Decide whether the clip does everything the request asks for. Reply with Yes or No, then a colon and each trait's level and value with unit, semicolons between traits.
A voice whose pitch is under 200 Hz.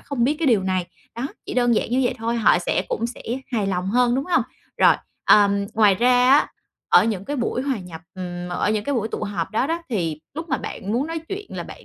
No: high, 230 Hz